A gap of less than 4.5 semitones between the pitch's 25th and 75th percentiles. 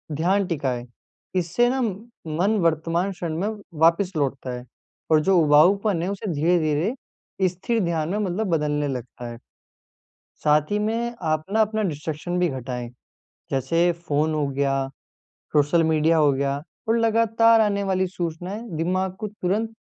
No: average, 5.1 semitones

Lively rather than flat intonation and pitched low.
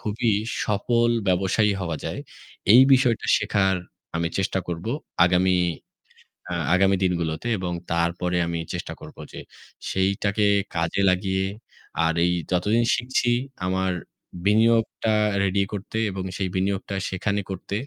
No: average, 2.7 semitones; very low, 95 Hz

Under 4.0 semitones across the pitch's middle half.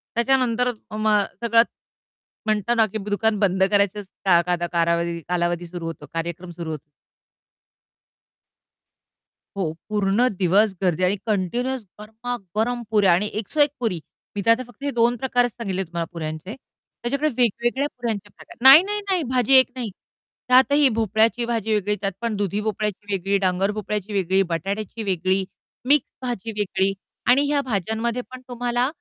No: average, 4.4 semitones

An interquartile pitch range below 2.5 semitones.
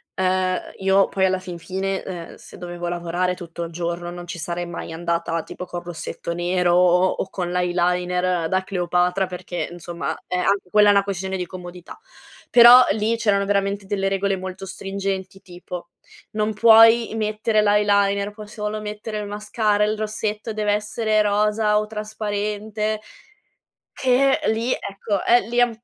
No: average, 2.9 semitones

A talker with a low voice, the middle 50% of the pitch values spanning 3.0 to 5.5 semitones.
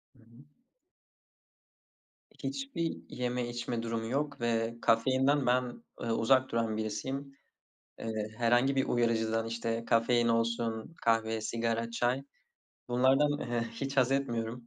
No: low, 120 Hz; narrow, 2.4 semitones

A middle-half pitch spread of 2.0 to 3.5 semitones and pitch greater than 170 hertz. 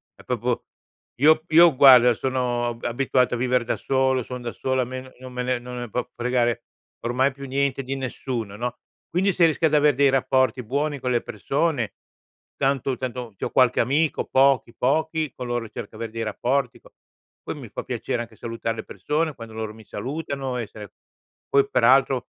No: narrow, 2.5 semitones; low, 130 Hz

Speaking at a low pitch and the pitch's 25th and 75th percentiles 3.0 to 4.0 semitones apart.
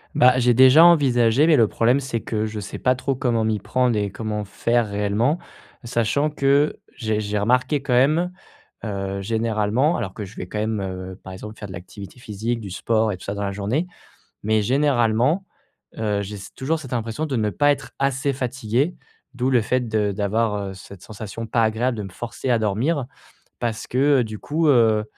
Yes: low, 115 Hz; average, 3.7 semitones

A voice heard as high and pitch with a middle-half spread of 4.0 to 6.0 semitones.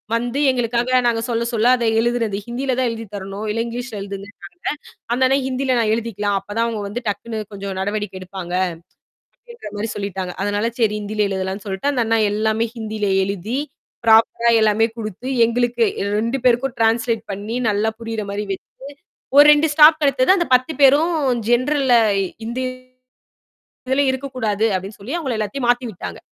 No: high, 230 Hz; average, 3.4 semitones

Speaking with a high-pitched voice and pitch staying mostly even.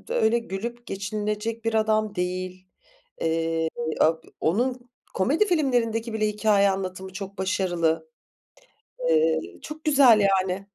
No: high, 210 Hz; average, 4.1 semitones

